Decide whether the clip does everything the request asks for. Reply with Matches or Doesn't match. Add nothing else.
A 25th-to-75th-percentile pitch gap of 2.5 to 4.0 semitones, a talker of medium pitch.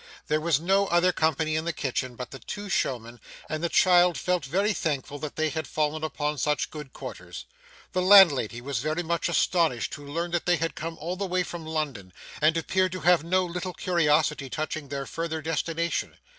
Matches